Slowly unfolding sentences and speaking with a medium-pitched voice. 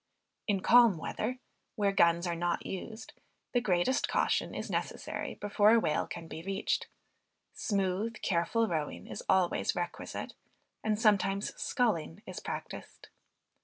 No: slow, 130 wpm; high, 195 Hz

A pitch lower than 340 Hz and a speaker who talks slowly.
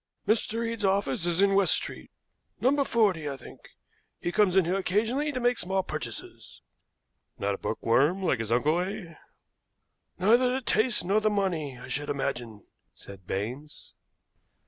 No: high, 190 Hz; average, 155 wpm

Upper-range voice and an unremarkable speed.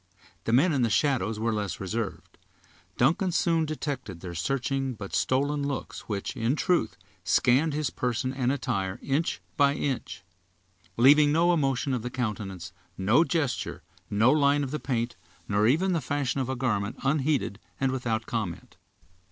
No: low, 130 Hz; average, 160 wpm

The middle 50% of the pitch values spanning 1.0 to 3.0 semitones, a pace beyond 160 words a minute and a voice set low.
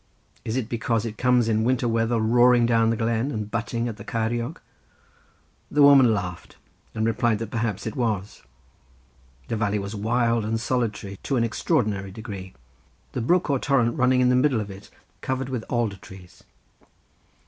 Yes: narrow, 2.5 semitones; average, 170 wpm; low, 115 Hz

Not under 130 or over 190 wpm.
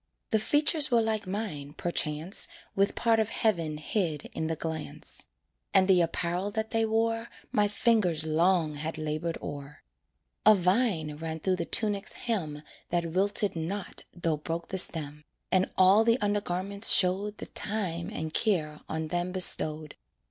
Yes: average, 155 wpm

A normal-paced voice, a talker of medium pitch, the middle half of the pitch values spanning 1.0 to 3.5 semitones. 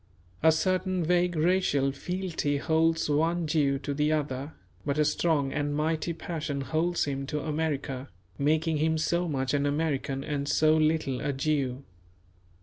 Yes: average, 150 wpm; medium, 155 Hz; narrow, 2.4 semitones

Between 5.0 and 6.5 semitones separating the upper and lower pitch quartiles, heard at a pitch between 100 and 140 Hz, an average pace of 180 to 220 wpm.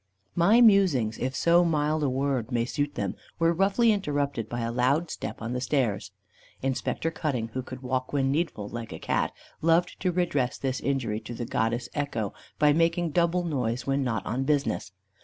Yes: wide, 5.4 semitones; low, 135 Hz; average, 185 wpm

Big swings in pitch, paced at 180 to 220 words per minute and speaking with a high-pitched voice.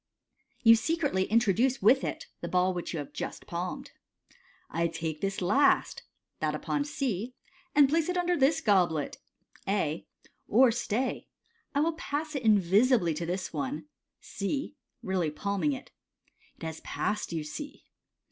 No: wide, 7.5 semitones; average, 160 wpm; high, 220 Hz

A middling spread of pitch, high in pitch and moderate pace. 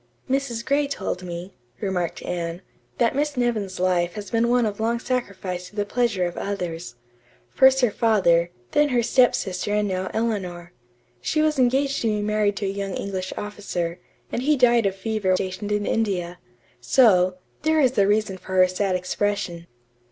Yes: average, 4.5 semitones; high, 205 Hz; average, 175 wpm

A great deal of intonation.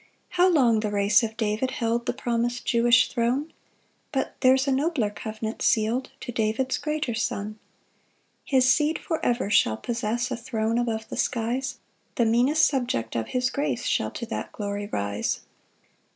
No: average, 3.1 semitones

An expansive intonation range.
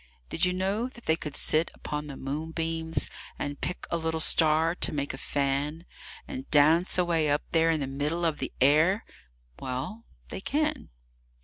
No: average, 3.1 semitones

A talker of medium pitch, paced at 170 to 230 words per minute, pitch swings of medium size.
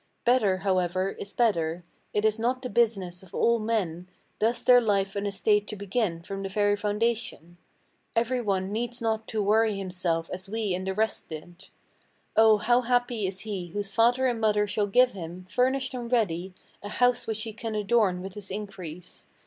No: high, 210 Hz; average, 185 wpm; average, 3.4 semitones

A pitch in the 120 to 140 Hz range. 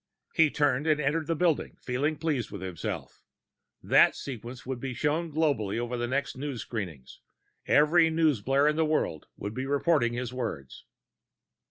Yes: low, 135 Hz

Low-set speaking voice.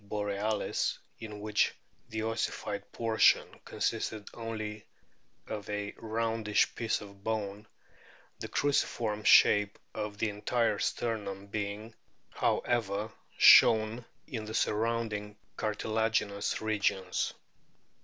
Yes: low, 110 Hz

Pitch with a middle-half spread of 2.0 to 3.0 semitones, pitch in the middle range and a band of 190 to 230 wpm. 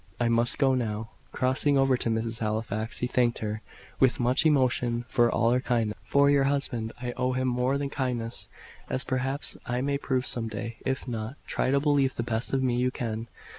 No: narrow, 2.4 semitones; low, 125 Hz; fast, 205 wpm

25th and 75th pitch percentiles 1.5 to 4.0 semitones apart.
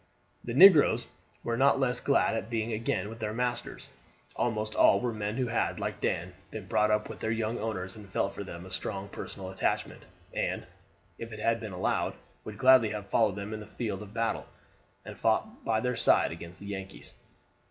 Yes: average, 2.7 semitones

